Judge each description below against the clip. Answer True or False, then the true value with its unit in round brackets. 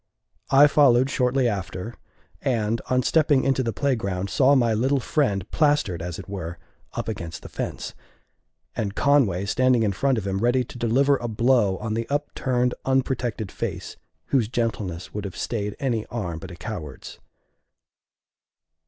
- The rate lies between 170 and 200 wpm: False (155 wpm)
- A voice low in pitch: True (115 Hz)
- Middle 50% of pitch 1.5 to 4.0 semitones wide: False (4.9 semitones)